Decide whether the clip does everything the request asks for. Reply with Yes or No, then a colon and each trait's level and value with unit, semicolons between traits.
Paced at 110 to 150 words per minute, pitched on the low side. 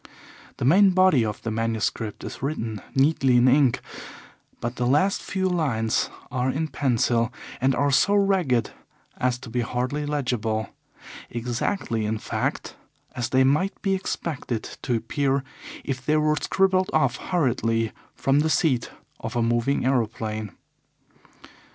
Yes: average, 140 wpm; low, 130 Hz